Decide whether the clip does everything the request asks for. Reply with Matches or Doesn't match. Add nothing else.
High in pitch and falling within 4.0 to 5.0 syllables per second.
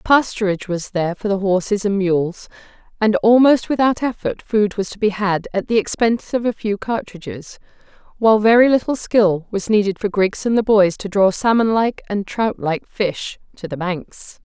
Matches